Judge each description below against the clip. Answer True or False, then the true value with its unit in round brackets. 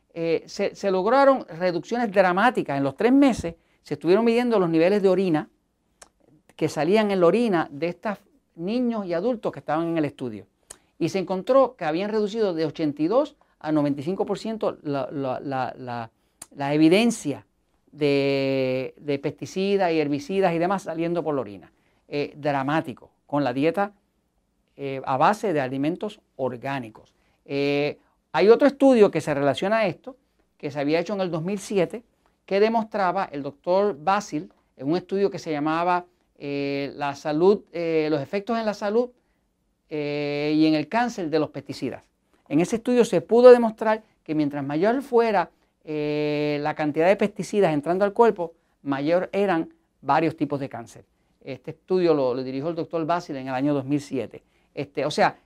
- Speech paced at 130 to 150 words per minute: False (165 wpm)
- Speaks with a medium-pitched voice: True (165 Hz)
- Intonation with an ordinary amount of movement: False (5.7 semitones)